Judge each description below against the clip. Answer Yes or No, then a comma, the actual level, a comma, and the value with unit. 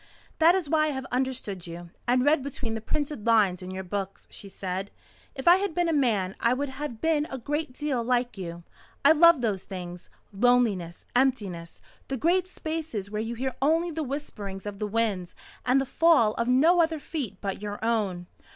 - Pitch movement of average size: No, wide, 6.9 semitones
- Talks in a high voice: Yes, high, 245 Hz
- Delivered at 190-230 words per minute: Yes, average, 195 wpm